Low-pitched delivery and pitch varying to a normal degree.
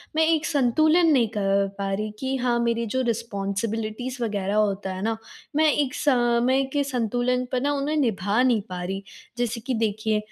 No: high, 235 Hz; average, 3.7 semitones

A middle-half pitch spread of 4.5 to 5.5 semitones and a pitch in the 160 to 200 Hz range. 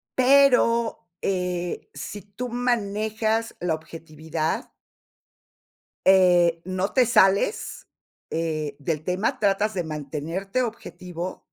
Yes: average, 5.0 semitones; high, 190 Hz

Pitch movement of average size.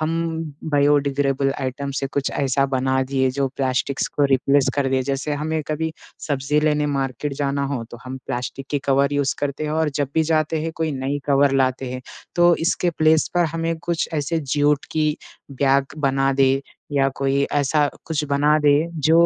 No: narrow, 2.0 semitones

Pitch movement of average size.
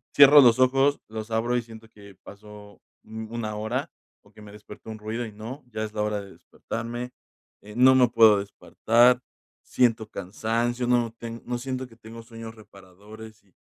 No: narrow, 2.2 semitones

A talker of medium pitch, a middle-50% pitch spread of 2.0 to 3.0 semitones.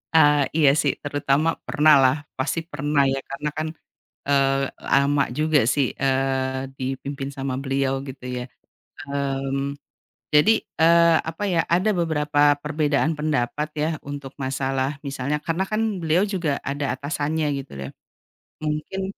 Yes: medium, 145 Hz; narrow, 2.5 semitones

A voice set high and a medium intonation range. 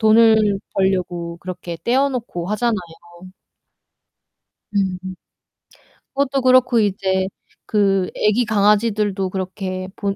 Yes: high, 200 Hz; average, 3.3 semitones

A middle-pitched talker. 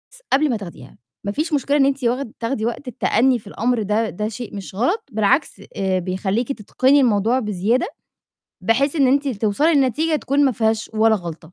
No: high, 230 Hz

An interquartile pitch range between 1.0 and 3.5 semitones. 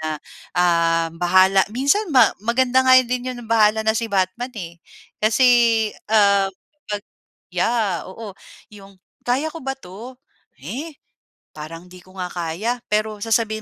No: average, 4.9 semitones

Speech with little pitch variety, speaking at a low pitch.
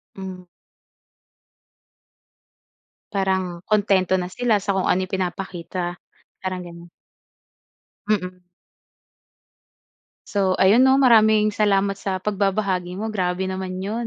No: narrow, 2.1 semitones; high, 190 Hz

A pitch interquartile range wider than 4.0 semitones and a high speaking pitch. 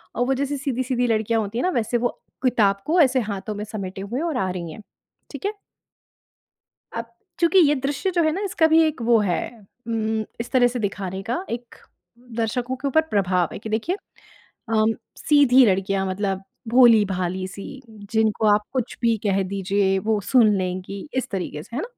Yes: average, 4.7 semitones; high, 225 Hz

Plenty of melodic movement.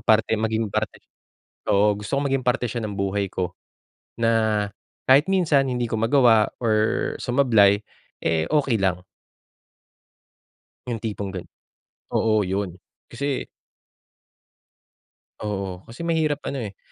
No: average, 4.3 semitones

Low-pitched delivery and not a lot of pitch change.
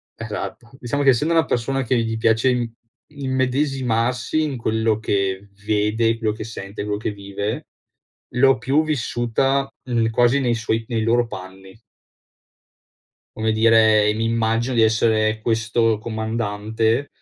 Yes: low, 115 Hz; narrow, 2.2 semitones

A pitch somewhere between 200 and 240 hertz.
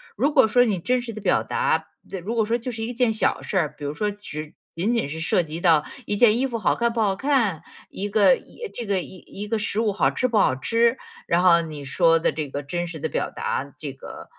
Yes: high, 205 Hz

